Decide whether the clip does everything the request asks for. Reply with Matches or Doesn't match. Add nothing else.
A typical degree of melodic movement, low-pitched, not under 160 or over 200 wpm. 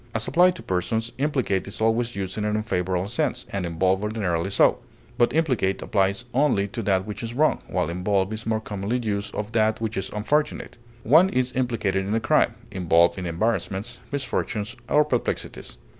Matches